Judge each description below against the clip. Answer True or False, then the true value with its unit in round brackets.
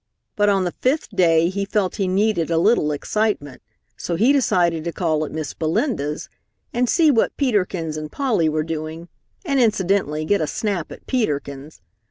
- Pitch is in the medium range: True (180 Hz)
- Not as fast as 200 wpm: True (185 wpm)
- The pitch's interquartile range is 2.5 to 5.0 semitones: False (5.4 semitones)